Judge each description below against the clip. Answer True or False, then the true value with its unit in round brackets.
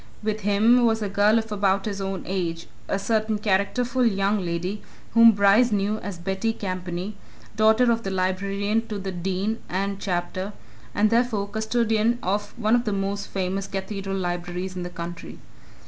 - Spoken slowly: False (165 wpm)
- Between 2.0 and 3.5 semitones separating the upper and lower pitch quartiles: True (2.4 semitones)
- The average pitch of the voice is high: True (200 Hz)